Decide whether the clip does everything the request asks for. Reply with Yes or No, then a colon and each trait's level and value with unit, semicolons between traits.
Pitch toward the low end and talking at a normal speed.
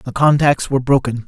Yes: low, 130 Hz; average, 190 wpm